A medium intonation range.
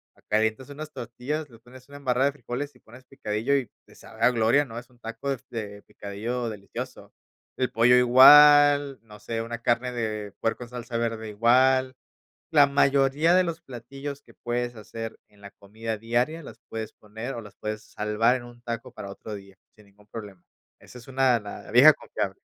Yes: average, 3.2 semitones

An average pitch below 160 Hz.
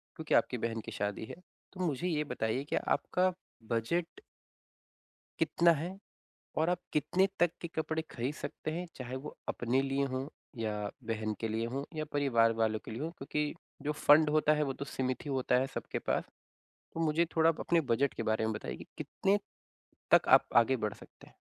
Yes: medium, 140 Hz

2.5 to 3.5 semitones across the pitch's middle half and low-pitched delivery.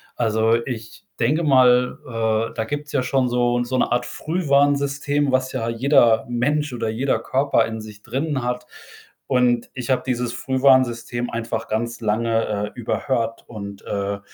Yes: average, 2.8 semitones; low, 125 Hz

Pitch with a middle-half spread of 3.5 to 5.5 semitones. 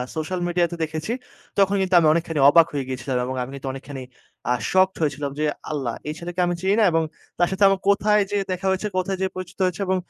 Yes: average, 4.3 semitones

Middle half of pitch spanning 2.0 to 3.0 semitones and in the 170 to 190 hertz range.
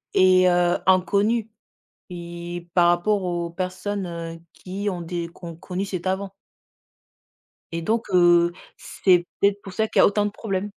Yes: narrow, 2.5 semitones; medium, 185 Hz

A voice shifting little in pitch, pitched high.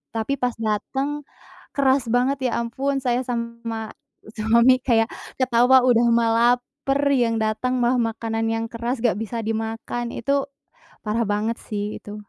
Yes: narrow, 2.2 semitones; high, 235 Hz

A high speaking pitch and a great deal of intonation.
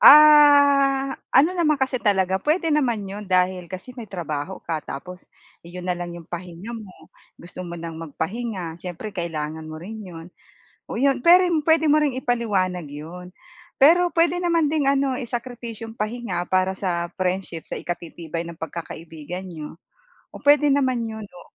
Yes: high, 195 Hz; wide, 7.8 semitones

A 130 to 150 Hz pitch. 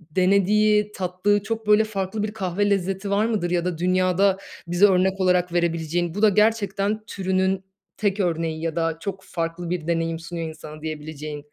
No: medium, 185 Hz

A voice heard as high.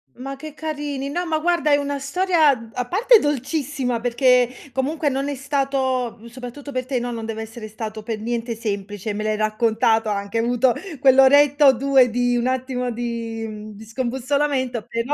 Yes: very high, 250 Hz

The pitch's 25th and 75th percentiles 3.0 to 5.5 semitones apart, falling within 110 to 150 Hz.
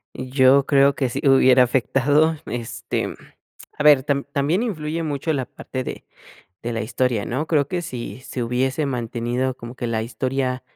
No: narrow, 2.6 semitones; low, 130 Hz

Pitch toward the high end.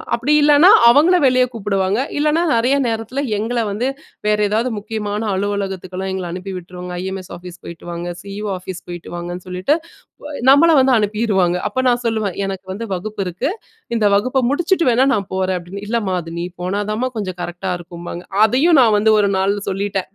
Yes: high, 205 Hz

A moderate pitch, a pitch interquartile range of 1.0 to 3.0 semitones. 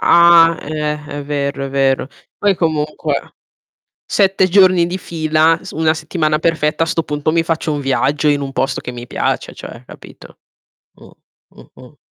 Yes: medium, 155 Hz; narrow, 2.4 semitones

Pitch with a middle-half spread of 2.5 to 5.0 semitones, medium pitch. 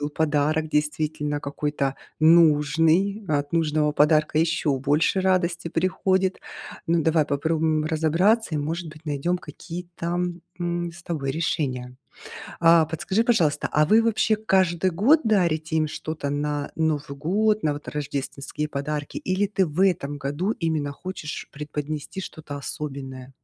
Yes: average, 2.9 semitones; medium, 155 Hz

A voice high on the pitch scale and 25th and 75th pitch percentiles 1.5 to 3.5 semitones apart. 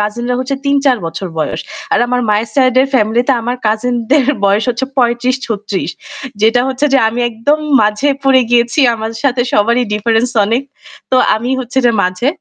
Yes: high, 240 Hz; average, 2.9 semitones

